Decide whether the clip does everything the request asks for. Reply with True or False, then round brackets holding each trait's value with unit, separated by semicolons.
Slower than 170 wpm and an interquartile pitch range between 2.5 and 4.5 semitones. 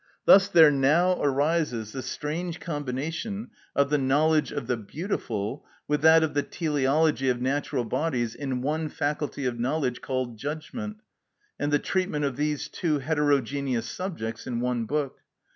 True (150 wpm; 3.7 semitones)